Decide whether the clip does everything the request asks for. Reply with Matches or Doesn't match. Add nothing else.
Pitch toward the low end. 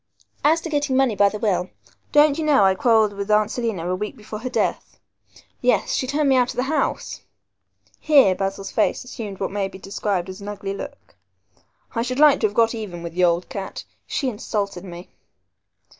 Doesn't match